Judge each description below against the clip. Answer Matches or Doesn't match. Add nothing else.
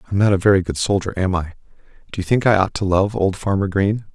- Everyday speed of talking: Doesn't match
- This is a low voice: Matches